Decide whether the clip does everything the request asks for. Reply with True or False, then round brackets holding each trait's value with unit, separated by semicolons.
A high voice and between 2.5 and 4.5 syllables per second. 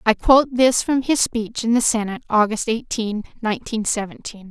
False (225 Hz; 5.4 syllables/s)